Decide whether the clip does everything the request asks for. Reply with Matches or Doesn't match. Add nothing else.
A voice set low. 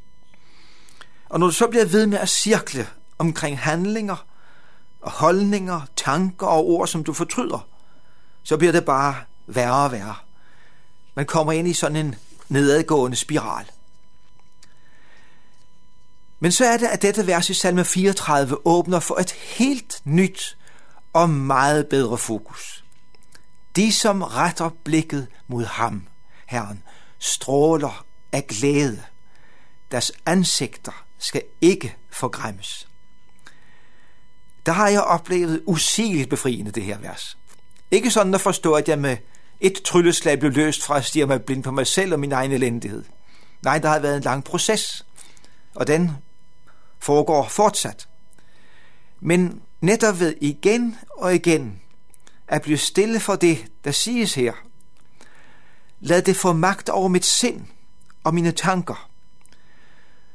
Doesn't match